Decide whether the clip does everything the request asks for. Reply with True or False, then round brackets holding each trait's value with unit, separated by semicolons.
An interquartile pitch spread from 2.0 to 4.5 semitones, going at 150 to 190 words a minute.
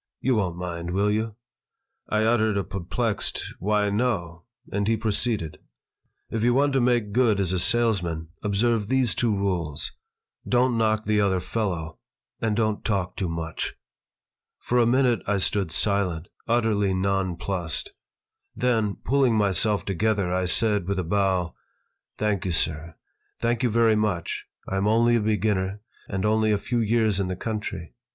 True (3.3 semitones; 160 wpm)